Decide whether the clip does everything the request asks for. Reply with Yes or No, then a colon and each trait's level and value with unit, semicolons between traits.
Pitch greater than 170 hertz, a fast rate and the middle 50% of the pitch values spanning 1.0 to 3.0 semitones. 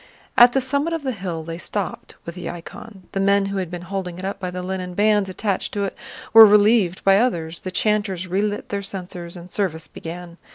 Yes: high, 190 Hz; fast, 215 wpm; narrow, 2.6 semitones